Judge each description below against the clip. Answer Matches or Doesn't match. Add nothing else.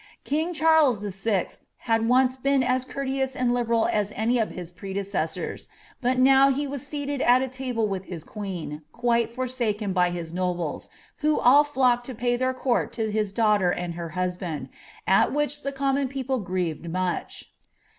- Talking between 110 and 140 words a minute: Doesn't match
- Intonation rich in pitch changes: Matches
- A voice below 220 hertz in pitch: Doesn't match